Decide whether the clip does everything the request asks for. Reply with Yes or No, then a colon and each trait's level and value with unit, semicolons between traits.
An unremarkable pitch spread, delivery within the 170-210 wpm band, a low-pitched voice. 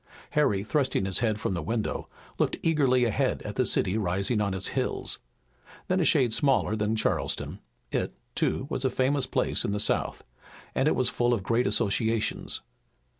Yes: average, 4.2 semitones; average, 175 wpm; low, 115 Hz